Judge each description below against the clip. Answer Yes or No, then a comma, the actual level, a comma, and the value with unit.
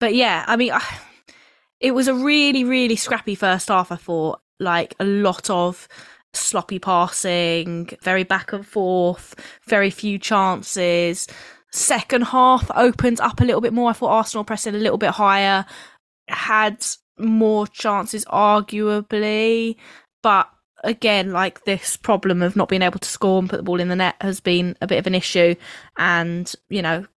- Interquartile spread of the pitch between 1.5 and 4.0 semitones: Yes, average, 3.5 semitones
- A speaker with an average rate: Yes, average, 165 wpm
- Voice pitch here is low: No, high, 200 Hz